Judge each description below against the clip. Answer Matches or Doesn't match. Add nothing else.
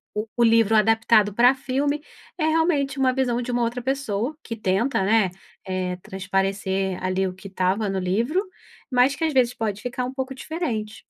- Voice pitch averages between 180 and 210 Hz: Doesn't match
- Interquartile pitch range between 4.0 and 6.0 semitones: Matches